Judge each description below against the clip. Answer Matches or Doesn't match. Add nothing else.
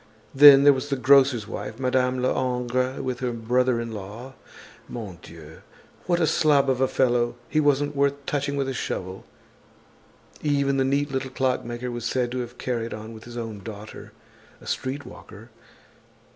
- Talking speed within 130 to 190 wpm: Matches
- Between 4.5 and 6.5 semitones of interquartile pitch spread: Doesn't match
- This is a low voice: Matches